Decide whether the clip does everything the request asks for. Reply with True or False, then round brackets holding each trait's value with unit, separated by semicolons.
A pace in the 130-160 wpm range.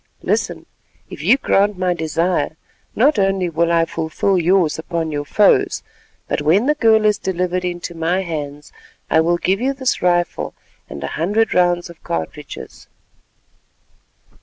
True (150 wpm)